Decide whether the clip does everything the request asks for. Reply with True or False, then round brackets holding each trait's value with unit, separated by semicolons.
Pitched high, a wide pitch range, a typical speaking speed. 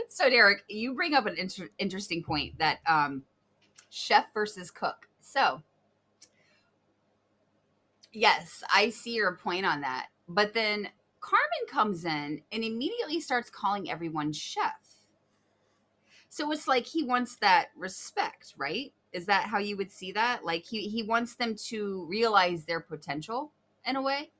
True (210 Hz; 6.0 semitones; 150 wpm)